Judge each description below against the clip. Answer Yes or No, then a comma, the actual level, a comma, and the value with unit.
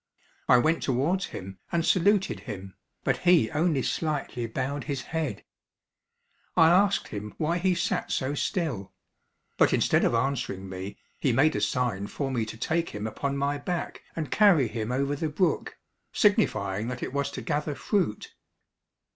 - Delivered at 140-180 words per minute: Yes, average, 165 wpm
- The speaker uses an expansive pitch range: Yes, wide, 6.3 semitones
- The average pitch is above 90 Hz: Yes, medium, 140 Hz